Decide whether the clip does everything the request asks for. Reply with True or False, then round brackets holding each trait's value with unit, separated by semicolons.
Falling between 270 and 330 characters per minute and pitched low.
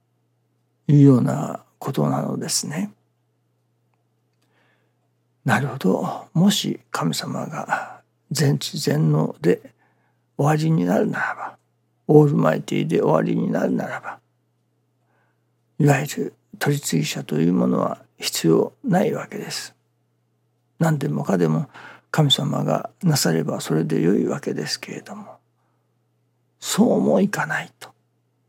False (230 characters per minute; 80 Hz)